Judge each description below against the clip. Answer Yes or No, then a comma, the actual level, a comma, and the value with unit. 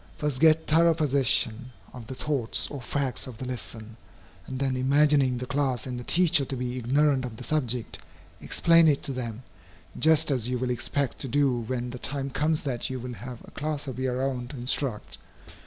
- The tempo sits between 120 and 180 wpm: No, average, 200 wpm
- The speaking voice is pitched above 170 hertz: No, low, 130 Hz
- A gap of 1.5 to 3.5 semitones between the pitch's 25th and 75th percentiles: Yes, average, 2.8 semitones